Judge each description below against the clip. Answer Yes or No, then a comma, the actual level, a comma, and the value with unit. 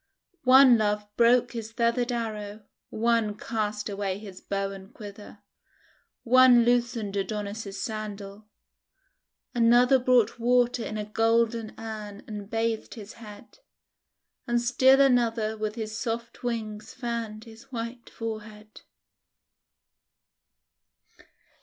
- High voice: Yes, high, 225 Hz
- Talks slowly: Yes, slow, 110 wpm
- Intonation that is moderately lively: No, narrow, 2.1 semitones